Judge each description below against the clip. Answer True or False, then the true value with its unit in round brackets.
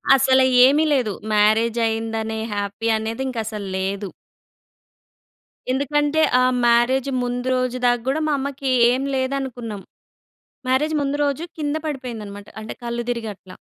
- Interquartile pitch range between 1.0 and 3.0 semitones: False (3.4 semitones)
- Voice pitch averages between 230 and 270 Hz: True (245 Hz)